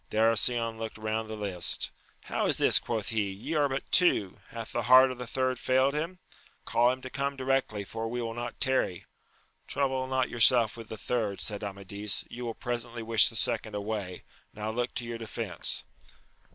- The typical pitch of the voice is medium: No, low, 115 Hz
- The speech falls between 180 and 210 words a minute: Yes, average, 190 wpm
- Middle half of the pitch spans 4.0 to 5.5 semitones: No, average, 3.0 semitones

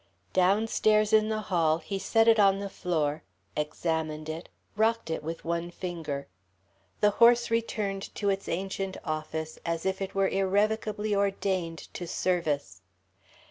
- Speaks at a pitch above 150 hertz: Yes, high, 190 Hz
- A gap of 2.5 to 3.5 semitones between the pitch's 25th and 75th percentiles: No, average, 4.2 semitones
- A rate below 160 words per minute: Yes, average, 140 wpm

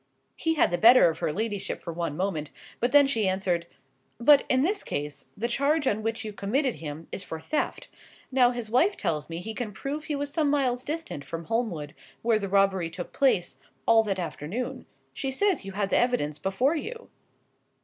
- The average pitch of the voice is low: No, high, 220 Hz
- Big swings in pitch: Yes, wide, 7.3 semitones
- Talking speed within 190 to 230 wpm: Yes, average, 200 wpm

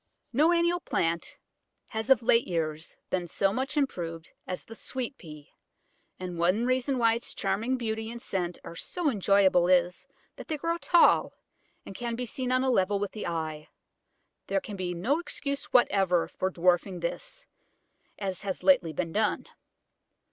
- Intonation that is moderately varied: No, wide, 6.4 semitones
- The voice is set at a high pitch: Yes, high, 205 Hz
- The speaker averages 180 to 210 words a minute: No, average, 165 wpm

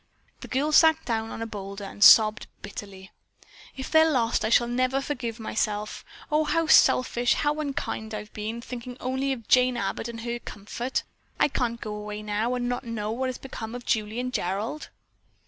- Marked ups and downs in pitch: No, average, 3.2 semitones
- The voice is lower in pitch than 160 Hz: No, high, 235 Hz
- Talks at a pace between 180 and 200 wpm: Yes, average, 190 wpm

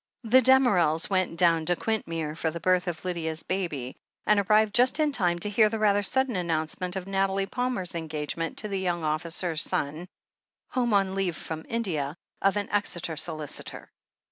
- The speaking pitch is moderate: Yes, medium, 180 Hz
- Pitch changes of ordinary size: Yes, average, 4.1 semitones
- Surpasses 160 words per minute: Yes, average, 170 wpm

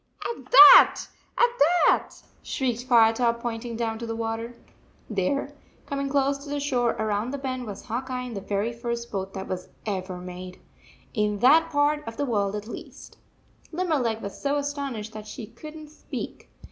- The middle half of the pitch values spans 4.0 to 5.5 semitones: Yes, average, 4.7 semitones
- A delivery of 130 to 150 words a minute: No, average, 185 wpm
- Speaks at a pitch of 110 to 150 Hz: No, high, 235 Hz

